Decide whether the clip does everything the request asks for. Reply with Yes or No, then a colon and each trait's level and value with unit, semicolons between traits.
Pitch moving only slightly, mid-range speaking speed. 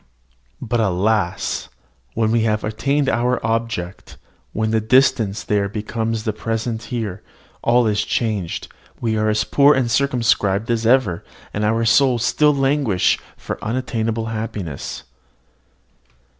No: narrow, 2.1 semitones; slow, 130 wpm